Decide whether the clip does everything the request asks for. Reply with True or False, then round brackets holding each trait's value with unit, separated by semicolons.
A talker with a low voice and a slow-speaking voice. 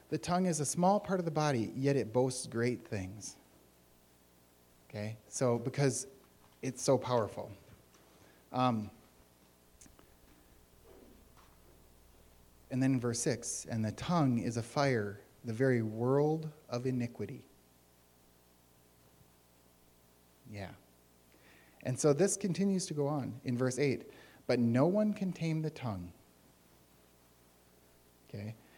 True (105 Hz; 115 wpm)